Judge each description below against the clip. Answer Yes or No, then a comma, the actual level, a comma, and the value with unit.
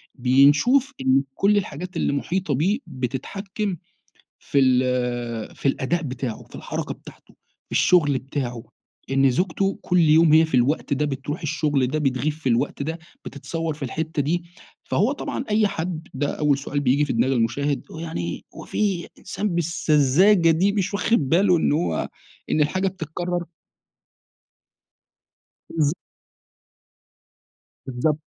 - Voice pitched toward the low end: No, medium, 150 Hz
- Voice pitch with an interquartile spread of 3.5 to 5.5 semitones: Yes, average, 4.7 semitones